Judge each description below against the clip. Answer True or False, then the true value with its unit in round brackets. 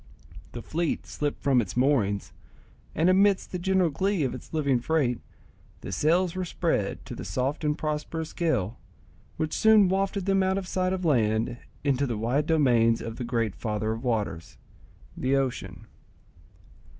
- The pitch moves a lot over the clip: True (7.1 semitones)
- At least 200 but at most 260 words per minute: False (160 wpm)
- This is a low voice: False (145 Hz)